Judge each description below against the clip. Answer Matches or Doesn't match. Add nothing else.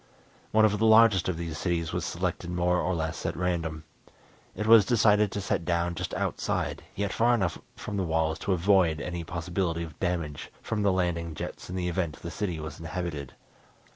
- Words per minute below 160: Doesn't match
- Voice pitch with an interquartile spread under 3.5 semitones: Matches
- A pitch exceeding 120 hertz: Doesn't match